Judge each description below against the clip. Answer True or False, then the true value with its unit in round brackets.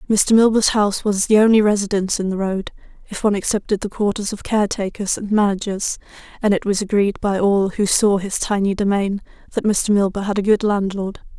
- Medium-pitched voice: False (200 Hz)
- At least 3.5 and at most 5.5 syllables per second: False (5.8 syllables/s)